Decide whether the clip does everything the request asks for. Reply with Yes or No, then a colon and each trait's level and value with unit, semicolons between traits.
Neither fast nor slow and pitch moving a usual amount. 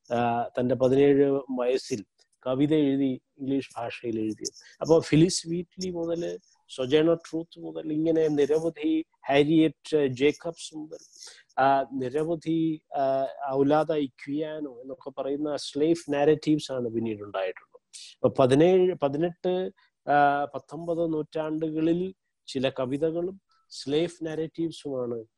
Yes: average, 85 wpm; average, 3.6 semitones